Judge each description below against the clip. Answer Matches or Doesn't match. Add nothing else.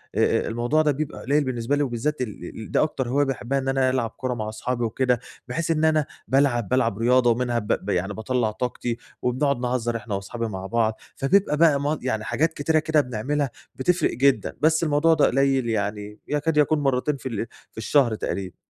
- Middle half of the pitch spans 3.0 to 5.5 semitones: Matches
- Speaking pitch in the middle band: Doesn't match